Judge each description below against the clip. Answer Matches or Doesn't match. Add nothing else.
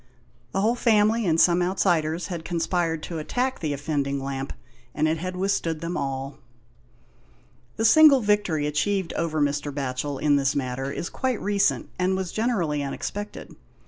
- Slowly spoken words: Doesn't match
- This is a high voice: Doesn't match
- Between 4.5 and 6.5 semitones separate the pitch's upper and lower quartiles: Matches